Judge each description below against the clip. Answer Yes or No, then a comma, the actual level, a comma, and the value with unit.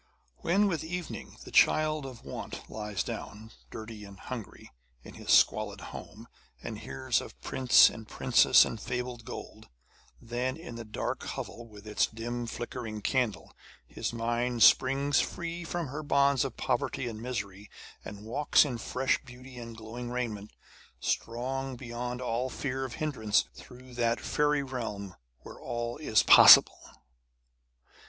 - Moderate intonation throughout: Yes, average, 3.0 semitones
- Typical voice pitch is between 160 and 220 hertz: No, low, 120 Hz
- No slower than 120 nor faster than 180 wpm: Yes, average, 145 wpm